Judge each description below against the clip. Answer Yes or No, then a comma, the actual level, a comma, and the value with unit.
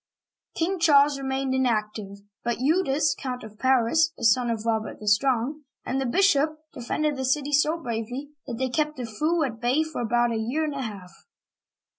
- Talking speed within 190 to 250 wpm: Yes, average, 195 wpm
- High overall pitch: Yes, very high, 260 Hz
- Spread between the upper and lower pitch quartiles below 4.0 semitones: No, average, 4.5 semitones